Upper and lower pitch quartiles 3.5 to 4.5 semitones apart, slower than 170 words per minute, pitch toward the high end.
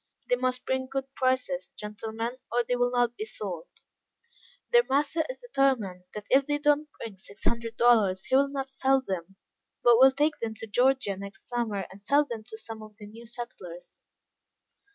No: average, 4.0 semitones; average, 190 wpm; high, 240 Hz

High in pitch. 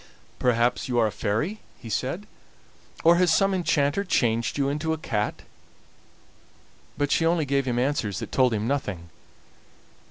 No: low, 135 Hz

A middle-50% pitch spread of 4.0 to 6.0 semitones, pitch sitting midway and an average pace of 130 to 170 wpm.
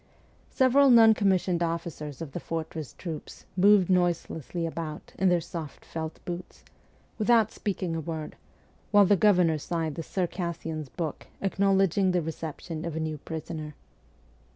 No: average, 3.2 semitones; medium, 170 Hz; average, 140 wpm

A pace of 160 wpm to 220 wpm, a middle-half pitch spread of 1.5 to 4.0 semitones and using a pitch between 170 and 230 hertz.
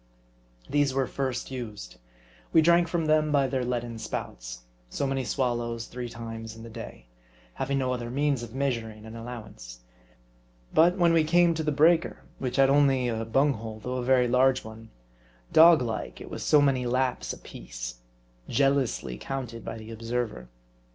No: average, 170 wpm; average, 3.6 semitones; low, 125 Hz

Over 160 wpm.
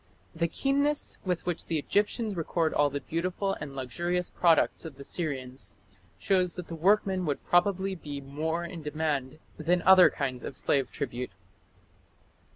No: average, 155 wpm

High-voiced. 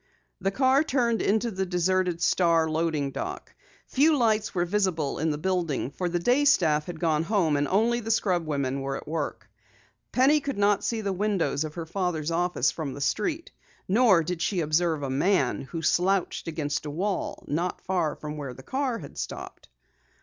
No: medium, 175 Hz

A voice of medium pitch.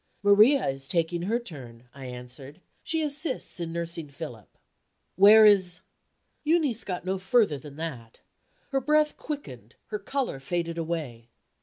Yes: medium, 170 Hz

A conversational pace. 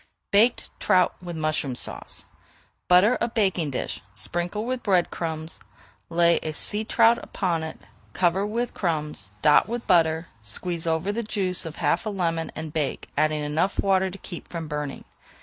Yes: average, 165 wpm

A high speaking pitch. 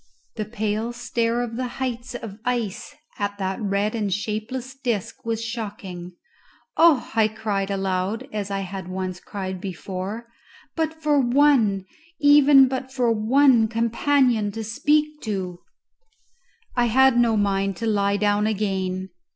Yes: high, 220 Hz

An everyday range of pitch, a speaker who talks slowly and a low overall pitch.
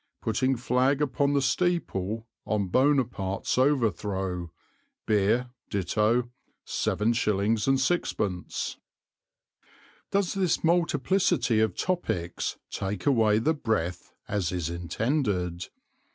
No: wide, 6.2 semitones; slow, 85 wpm; low, 115 Hz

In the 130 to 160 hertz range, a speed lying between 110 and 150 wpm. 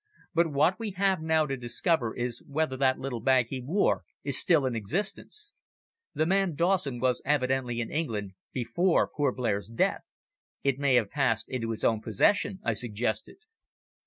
No: low, 135 Hz; average, 160 wpm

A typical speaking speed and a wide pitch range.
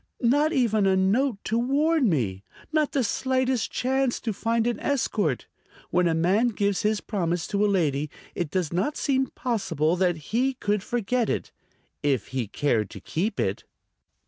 Yes: average, 170 wpm; wide, 6.7 semitones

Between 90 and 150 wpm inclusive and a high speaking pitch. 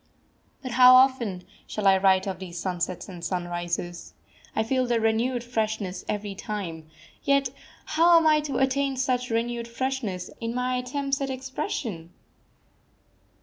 Yes: average, 145 wpm; high, 235 Hz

